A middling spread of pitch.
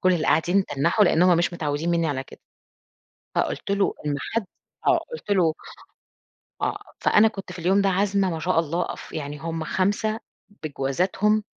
Yes: average, 3.7 semitones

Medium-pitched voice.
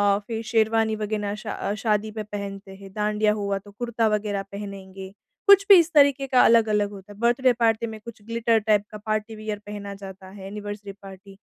No: high, 210 Hz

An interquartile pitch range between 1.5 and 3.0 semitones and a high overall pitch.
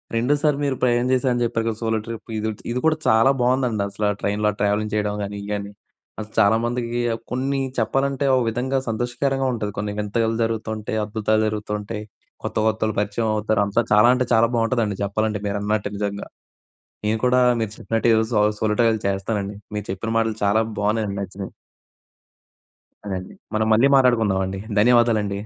No: narrow, 2.5 semitones; low, 110 Hz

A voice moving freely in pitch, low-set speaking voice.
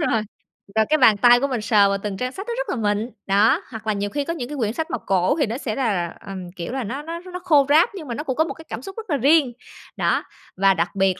No: wide, 6.6 semitones; high, 245 Hz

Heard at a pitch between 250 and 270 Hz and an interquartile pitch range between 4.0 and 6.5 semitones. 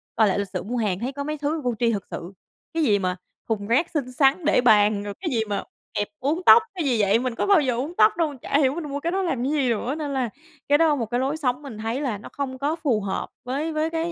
Yes: very high, 265 Hz; wide, 5.4 semitones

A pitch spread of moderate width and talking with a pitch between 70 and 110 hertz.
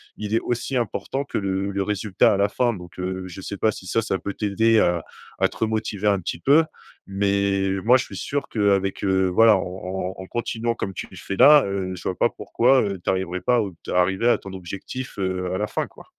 Yes: average, 3.1 semitones; low, 100 Hz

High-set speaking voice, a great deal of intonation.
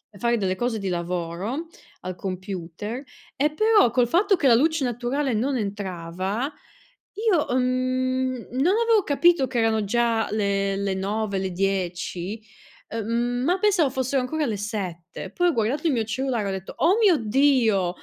Yes: high, 235 Hz; wide, 5.8 semitones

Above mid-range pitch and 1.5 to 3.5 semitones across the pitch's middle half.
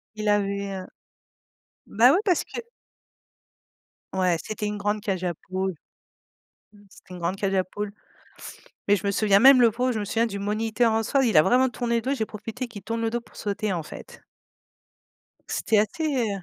Yes: high, 210 Hz; average, 2.9 semitones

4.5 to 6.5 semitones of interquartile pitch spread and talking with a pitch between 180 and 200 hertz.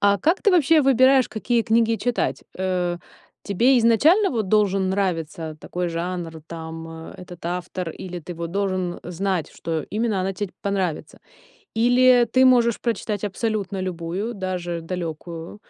Yes: average, 4.8 semitones; high, 190 Hz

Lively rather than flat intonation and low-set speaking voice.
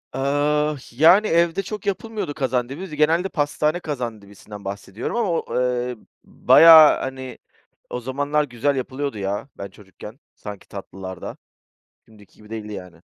Yes: wide, 6.2 semitones; low, 130 Hz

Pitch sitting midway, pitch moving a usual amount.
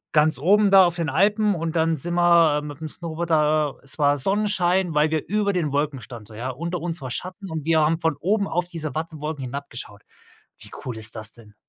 Yes: medium, 160 Hz; average, 3.5 semitones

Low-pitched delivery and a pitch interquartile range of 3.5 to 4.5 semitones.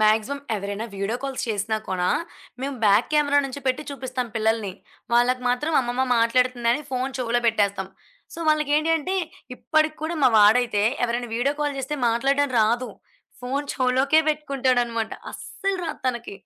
No: very high, 250 Hz; average, 3.9 semitones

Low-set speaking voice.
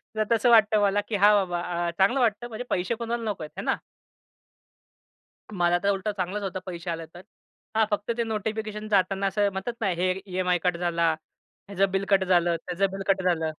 No: high, 195 Hz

